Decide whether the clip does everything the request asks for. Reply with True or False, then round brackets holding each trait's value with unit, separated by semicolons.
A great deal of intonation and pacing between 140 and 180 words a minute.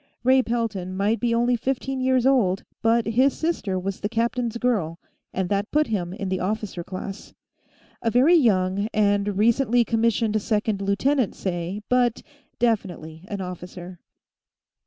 False (4.1 semitones; 145 wpm)